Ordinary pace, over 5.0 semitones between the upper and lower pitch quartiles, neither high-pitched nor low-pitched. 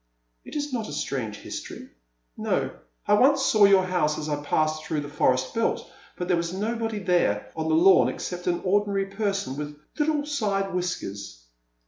Yes: average, 180 wpm; wide, 5.6 semitones; medium, 180 Hz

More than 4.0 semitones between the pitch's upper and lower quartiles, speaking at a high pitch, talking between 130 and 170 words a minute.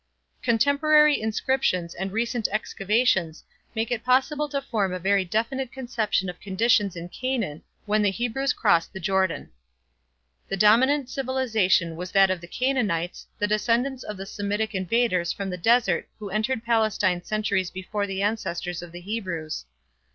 Yes: average, 4.4 semitones; high, 210 Hz; average, 150 wpm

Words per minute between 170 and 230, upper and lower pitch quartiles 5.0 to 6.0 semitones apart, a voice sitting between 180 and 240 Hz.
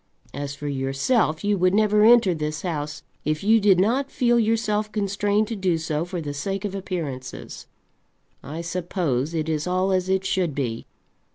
Yes: average, 175 wpm; average, 5.3 semitones; medium, 185 Hz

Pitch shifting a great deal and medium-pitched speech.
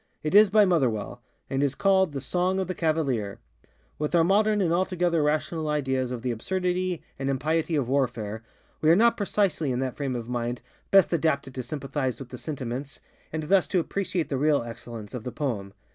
Yes: wide, 5.7 semitones; medium, 150 Hz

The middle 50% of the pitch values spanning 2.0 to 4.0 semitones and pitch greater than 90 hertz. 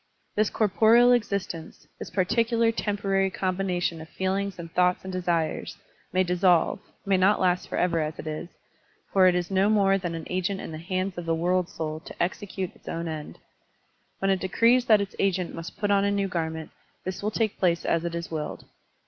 Yes: average, 2.8 semitones; medium, 185 Hz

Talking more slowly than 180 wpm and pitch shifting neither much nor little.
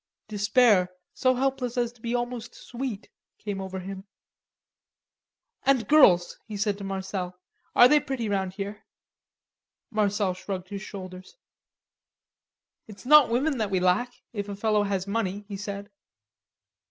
Yes: average, 140 wpm; average, 3.8 semitones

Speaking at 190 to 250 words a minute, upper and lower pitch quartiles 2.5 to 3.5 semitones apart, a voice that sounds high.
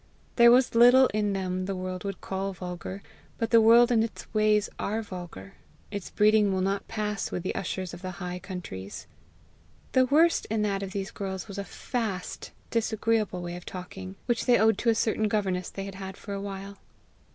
Yes: average, 195 wpm; average, 2.9 semitones; high, 200 Hz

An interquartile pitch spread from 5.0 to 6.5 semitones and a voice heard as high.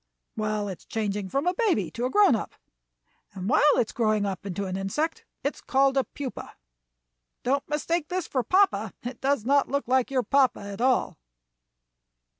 Yes: average, 5.3 semitones; very high, 255 Hz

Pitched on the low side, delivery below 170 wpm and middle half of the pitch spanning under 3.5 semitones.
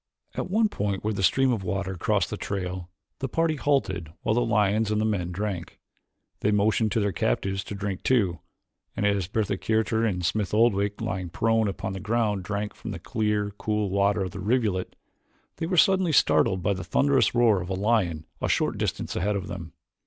No: low, 105 Hz; average, 200 wpm; average, 2.8 semitones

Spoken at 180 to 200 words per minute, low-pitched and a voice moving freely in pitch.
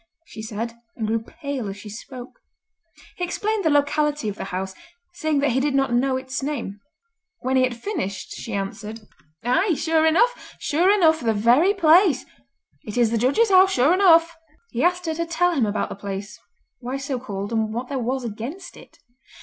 No: average, 190 wpm; very high, 265 Hz; wide, 6.5 semitones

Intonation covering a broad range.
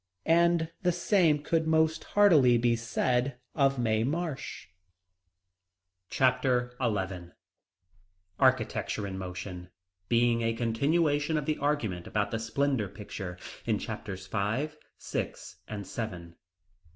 Yes: wide, 6.3 semitones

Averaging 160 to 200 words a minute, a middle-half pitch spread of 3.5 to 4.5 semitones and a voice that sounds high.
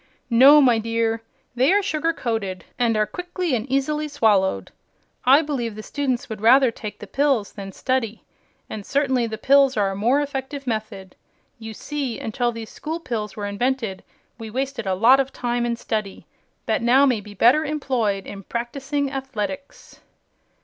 Yes: average, 170 wpm; average, 4.1 semitones; high, 240 Hz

